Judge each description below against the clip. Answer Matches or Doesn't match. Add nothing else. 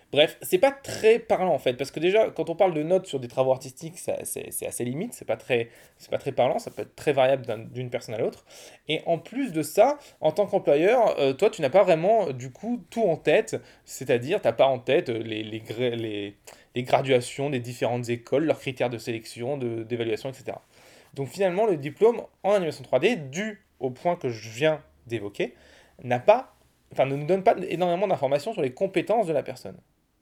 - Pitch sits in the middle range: Matches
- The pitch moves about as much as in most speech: Doesn't match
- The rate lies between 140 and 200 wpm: Doesn't match